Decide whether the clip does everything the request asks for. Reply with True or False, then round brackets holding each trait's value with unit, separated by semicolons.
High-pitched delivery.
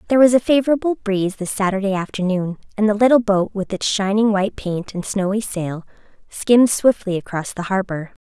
True (205 Hz)